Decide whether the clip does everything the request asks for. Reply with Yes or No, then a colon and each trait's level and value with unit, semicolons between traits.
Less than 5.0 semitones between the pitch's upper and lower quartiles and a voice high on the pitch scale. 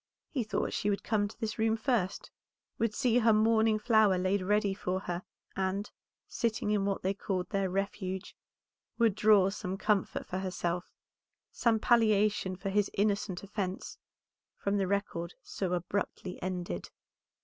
Yes: narrow, 2.4 semitones; high, 200 Hz